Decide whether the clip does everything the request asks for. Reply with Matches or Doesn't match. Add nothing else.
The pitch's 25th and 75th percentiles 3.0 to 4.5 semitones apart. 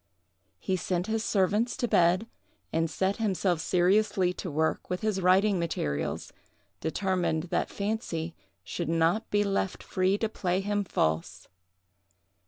Matches